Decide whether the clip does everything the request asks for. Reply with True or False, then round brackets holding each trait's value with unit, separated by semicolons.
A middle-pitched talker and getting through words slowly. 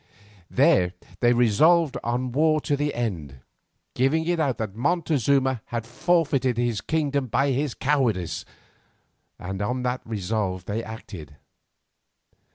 False (125 Hz; 125 wpm)